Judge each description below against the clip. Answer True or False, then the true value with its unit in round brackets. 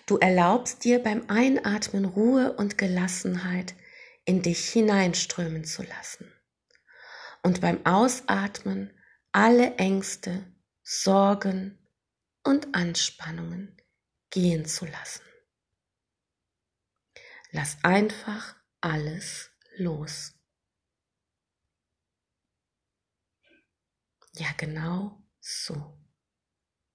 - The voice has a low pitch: False (180 Hz)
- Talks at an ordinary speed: False (70 wpm)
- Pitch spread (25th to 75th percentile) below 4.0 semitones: False (4.8 semitones)